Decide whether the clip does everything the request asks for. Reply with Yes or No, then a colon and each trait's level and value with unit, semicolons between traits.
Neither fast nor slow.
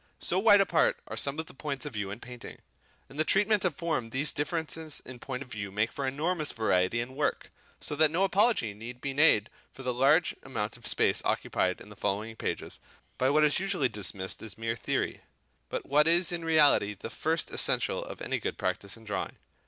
No: fast, 215 wpm